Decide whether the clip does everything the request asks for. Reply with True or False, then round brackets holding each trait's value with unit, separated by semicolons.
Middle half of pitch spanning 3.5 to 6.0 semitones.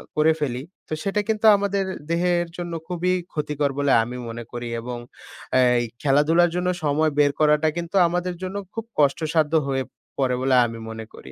True (4.6 semitones)